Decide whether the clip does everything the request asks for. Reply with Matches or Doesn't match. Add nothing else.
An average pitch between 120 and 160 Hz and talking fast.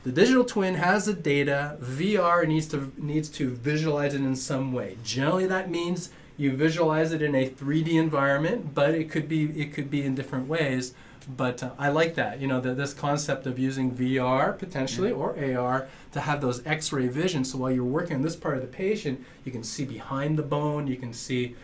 Matches